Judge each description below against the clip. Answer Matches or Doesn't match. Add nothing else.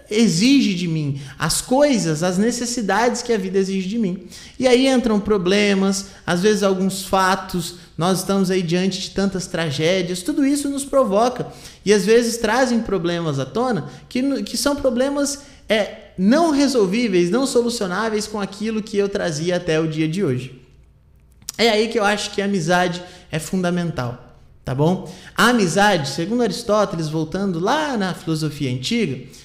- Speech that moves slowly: Doesn't match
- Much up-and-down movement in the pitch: Doesn't match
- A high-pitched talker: Matches